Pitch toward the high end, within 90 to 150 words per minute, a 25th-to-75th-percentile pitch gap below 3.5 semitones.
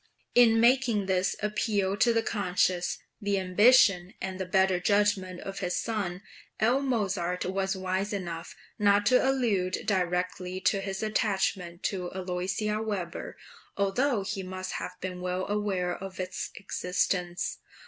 Yes: high, 195 Hz; average, 140 wpm; narrow, 2.5 semitones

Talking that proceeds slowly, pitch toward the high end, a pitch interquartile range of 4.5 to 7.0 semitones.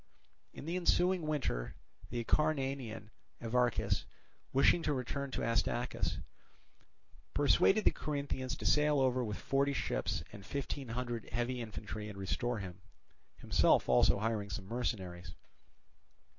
No: slow, 125 wpm; low, 120 Hz; average, 4.8 semitones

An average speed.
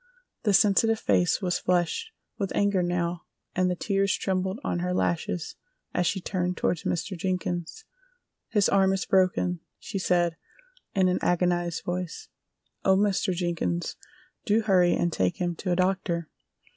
Yes: average, 150 wpm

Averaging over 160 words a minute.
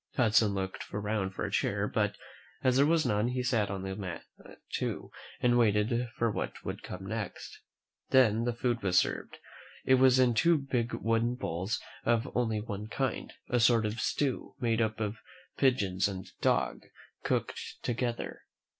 Yes: average, 175 wpm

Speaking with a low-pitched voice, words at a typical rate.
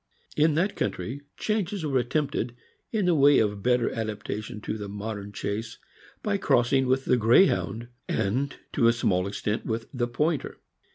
Yes: low, 120 Hz; average, 160 wpm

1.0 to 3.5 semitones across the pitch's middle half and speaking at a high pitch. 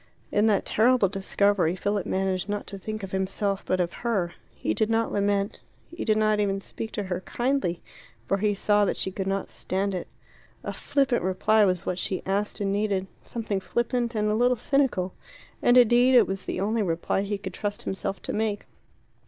Yes: narrow, 2.4 semitones; high, 205 Hz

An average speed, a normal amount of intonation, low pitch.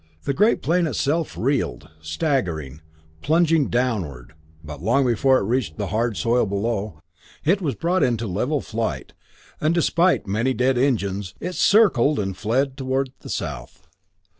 No: average, 145 wpm; wide, 6.4 semitones; low, 125 Hz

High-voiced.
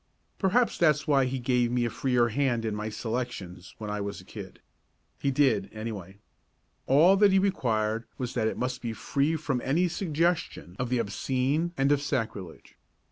No: low, 125 Hz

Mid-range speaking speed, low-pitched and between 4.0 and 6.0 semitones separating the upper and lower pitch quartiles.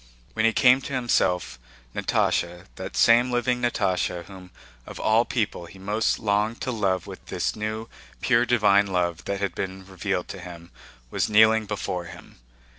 No: average, 165 wpm; low, 100 Hz; average, 3.5 semitones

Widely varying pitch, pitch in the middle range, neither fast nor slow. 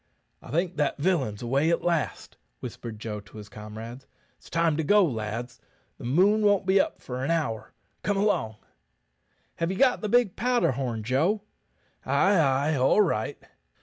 Yes: wide, 8.3 semitones; medium, 150 Hz; average, 170 wpm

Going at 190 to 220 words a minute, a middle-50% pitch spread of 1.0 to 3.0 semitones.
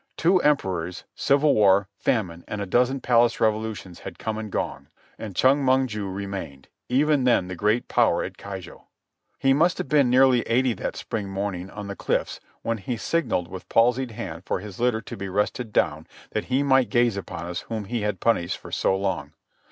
No: average, 195 wpm; average, 4.7 semitones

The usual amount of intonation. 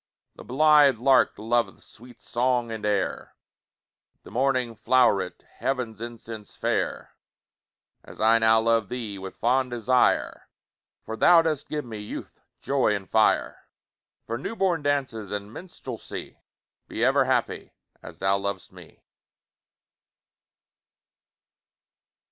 Yes: average, 3.3 semitones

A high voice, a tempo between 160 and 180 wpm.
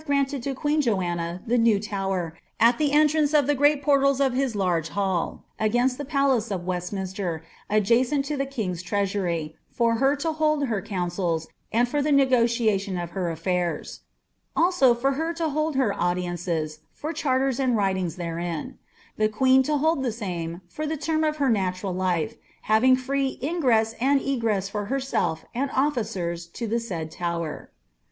Yes: high, 230 Hz; average, 170 wpm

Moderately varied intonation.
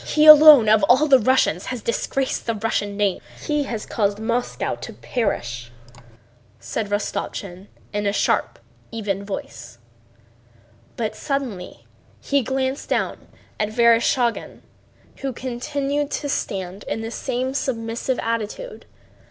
Yes: average, 4.4 semitones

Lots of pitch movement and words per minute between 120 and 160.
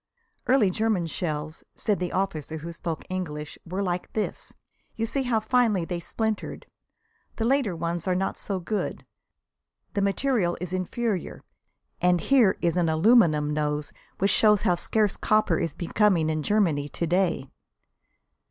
No: average, 4.5 semitones; average, 150 wpm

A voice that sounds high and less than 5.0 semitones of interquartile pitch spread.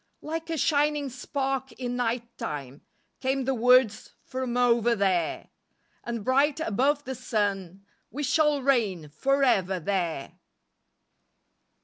No: high, 245 Hz; average, 5.3 semitones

